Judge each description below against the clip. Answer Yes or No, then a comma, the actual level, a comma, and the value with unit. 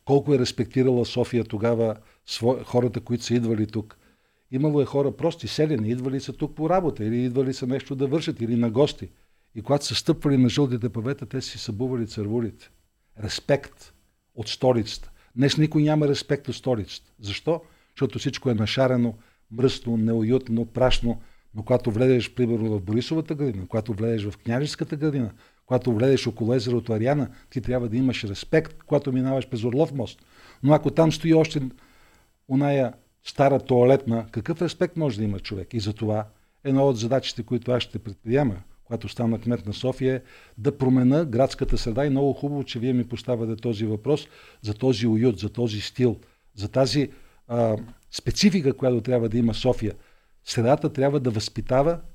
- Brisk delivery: Yes, fast, 170 wpm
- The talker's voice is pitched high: No, low, 125 Hz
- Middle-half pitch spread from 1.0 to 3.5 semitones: Yes, average, 3.2 semitones